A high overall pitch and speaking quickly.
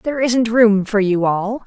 Yes: high, 220 Hz; fast, 215 wpm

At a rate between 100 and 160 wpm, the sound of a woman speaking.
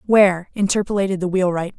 Yes: slow, 135 wpm; female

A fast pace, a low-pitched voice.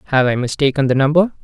No: fast, 210 wpm; medium, 145 Hz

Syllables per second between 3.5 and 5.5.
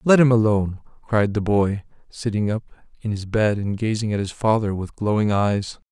Yes: 4.9 syllables/s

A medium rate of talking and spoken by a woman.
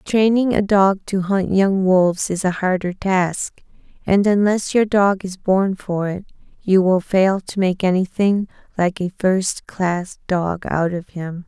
Yes: average, 170 wpm; female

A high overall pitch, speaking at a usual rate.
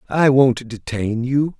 No: low, 130 Hz; average, 150 wpm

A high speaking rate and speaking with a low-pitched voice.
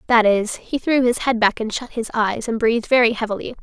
No: fast, 250 wpm; high, 230 Hz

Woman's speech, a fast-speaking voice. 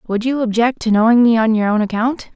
Yes: female; fast, 255 wpm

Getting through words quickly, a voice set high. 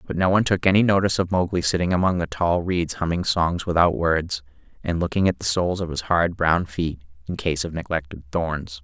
No: fast, 215 wpm; very low, 85 Hz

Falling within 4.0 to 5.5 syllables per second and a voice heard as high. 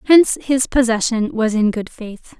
Yes: 4.6 syllables/s; high, 240 Hz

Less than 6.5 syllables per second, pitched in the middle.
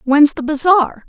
No: 3.9 syllables/s; very high, 295 Hz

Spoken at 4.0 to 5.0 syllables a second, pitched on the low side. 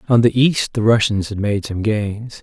Yes: 4.4 syllables/s; low, 110 Hz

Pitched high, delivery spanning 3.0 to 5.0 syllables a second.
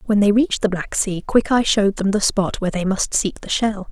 No: high, 205 Hz; 5.7 syllables/s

